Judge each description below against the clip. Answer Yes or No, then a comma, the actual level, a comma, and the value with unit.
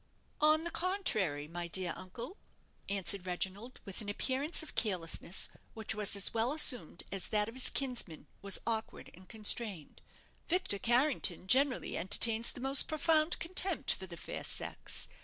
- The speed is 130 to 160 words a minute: Yes, average, 155 wpm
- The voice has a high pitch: Yes, high, 220 Hz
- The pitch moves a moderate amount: No, wide, 6.6 semitones